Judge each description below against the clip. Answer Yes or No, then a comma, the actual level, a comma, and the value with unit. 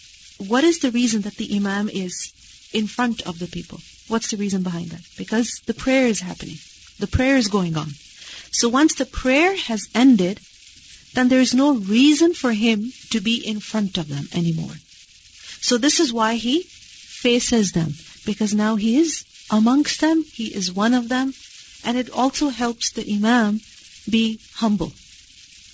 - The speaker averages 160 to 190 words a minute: Yes, average, 175 wpm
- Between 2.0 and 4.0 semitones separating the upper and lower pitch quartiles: No, average, 4.4 semitones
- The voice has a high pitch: Yes, high, 225 Hz